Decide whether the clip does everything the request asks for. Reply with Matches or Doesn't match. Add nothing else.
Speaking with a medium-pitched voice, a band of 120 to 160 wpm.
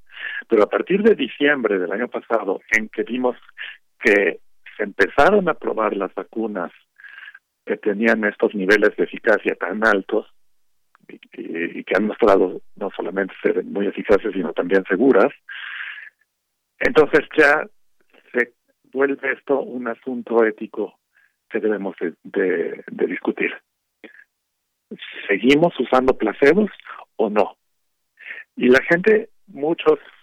Matches